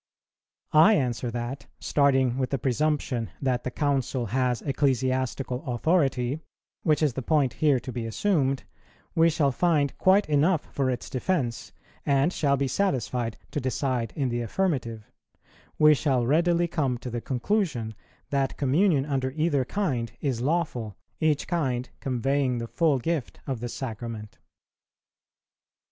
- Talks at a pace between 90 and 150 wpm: Yes, average, 140 wpm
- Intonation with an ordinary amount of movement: Yes, average, 3.7 semitones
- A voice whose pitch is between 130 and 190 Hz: Yes, low, 135 Hz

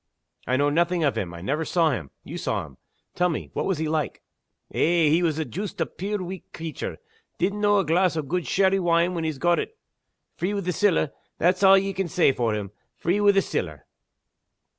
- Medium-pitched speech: Yes, medium, 170 Hz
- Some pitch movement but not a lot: Yes, average, 3.7 semitones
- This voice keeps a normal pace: No, fast, 215 wpm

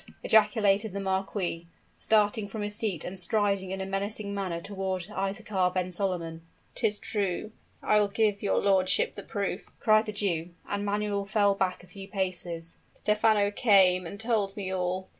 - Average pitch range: No, narrow, 2.0 semitones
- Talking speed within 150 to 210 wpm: Yes, average, 165 wpm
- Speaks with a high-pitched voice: Yes, high, 200 Hz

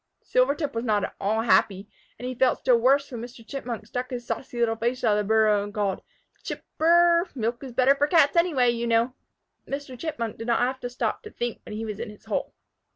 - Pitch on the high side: Yes, high, 240 Hz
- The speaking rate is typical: No, fast, 240 wpm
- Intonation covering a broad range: No, average, 3.1 semitones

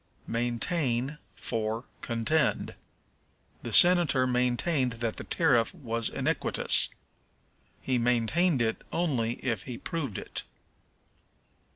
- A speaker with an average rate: No, slow, 95 wpm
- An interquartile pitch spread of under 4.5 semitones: No, average, 4.8 semitones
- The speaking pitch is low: Yes, low, 125 Hz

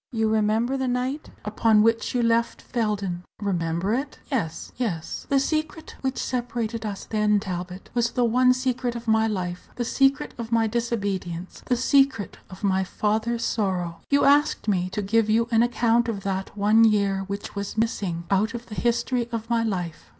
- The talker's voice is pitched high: Yes, high, 225 Hz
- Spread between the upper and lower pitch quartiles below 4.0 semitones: Yes, average, 3.3 semitones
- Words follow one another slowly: No, average, 180 wpm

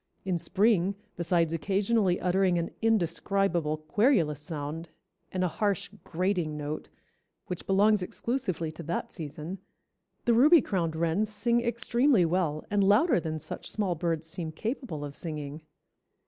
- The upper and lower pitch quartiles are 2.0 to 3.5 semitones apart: No, average, 4.3 semitones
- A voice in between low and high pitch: Yes, medium, 180 Hz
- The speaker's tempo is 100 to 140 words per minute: Yes, slow, 135 wpm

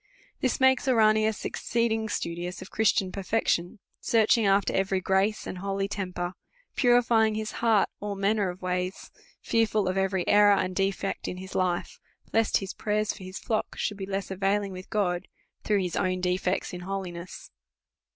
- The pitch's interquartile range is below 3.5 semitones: Yes, narrow, 2.6 semitones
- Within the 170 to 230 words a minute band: No, average, 160 wpm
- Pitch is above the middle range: Yes, high, 195 Hz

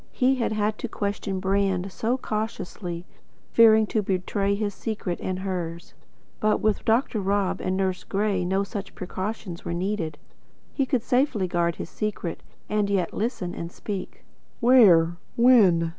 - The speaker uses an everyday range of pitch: Yes, average, 3.1 semitones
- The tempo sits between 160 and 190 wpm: No, average, 150 wpm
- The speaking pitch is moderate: No, high, 200 Hz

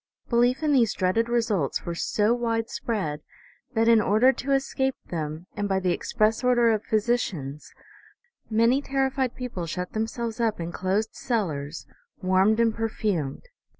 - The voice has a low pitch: No, high, 220 Hz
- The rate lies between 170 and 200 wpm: No, average, 150 wpm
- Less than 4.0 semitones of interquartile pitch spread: No, average, 4.4 semitones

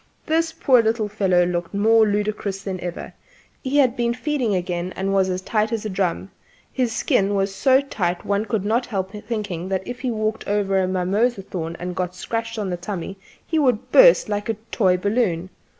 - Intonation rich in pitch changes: No, average, 3.5 semitones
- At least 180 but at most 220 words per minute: Yes, average, 200 wpm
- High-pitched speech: Yes, high, 205 Hz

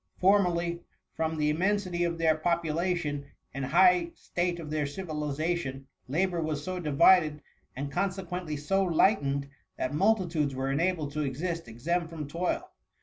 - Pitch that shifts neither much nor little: Yes, average, 3.3 semitones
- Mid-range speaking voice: Yes, medium, 165 Hz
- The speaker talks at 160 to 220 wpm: No, average, 150 wpm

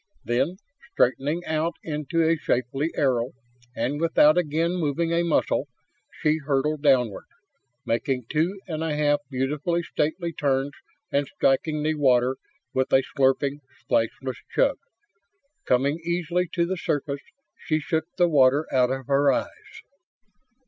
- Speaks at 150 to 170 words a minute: No, slow, 135 wpm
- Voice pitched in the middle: Yes, medium, 150 Hz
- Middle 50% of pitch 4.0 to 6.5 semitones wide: No, average, 3.6 semitones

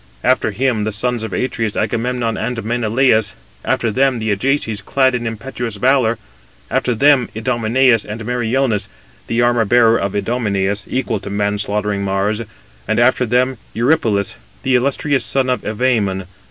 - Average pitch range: Yes, average, 3.1 semitones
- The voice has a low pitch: Yes, low, 115 Hz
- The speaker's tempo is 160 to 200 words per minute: No, average, 150 wpm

